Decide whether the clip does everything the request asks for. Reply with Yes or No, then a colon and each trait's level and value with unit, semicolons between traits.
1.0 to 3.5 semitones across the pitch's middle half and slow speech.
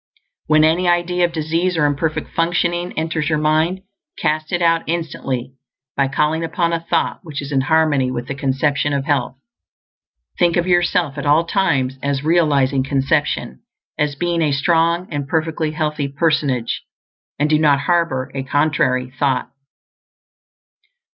No: average, 3.1 semitones; average, 150 wpm